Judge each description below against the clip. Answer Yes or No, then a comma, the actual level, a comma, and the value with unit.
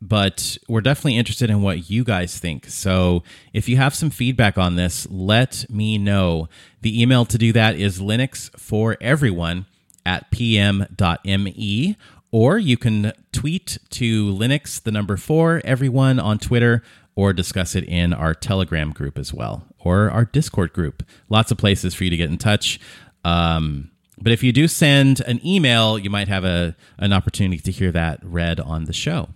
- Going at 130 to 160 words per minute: No, average, 175 wpm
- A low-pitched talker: Yes, low, 105 Hz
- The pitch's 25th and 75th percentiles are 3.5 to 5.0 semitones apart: Yes, average, 4.7 semitones